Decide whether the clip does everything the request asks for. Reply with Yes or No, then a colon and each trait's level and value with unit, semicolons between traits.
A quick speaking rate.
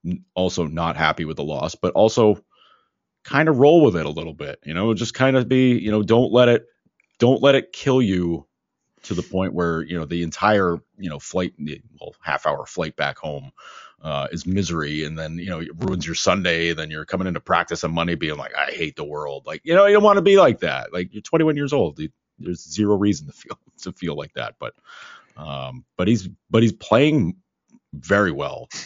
Yes: fast, 220 wpm